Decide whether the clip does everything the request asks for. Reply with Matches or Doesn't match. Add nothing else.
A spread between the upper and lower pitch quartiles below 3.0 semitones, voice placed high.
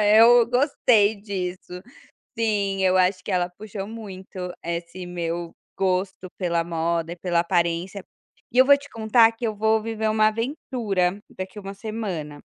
Doesn't match